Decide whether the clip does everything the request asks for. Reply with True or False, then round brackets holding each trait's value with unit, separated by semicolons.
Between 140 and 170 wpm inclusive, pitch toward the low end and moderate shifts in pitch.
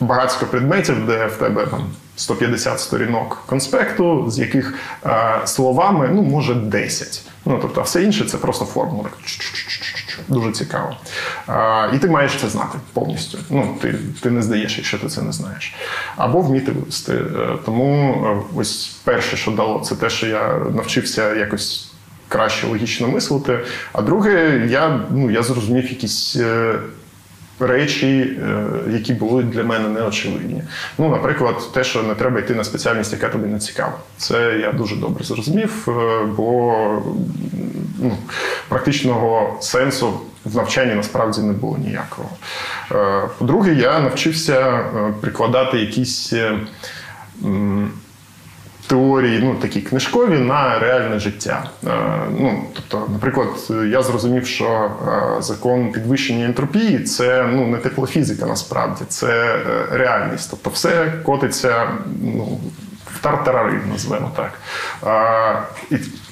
False (130 wpm; 125 Hz; 3.2 semitones)